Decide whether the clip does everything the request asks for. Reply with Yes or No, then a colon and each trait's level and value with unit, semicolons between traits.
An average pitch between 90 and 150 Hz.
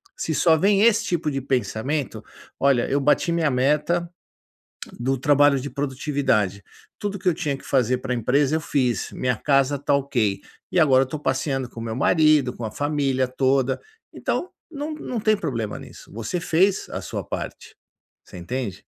Yes: medium, 140 Hz